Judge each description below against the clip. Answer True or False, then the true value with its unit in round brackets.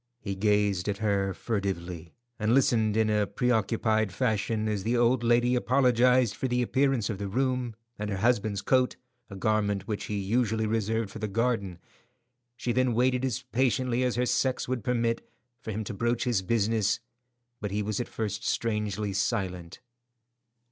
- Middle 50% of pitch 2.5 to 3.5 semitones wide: True (3.1 semitones)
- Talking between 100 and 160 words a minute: False (170 wpm)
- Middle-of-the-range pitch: False (110 Hz)